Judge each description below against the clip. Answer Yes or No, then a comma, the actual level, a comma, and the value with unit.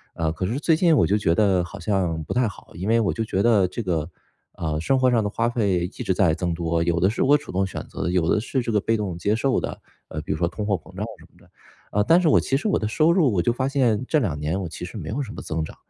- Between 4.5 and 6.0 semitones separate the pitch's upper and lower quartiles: Yes, wide, 5.5 semitones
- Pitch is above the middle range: No, low, 100 Hz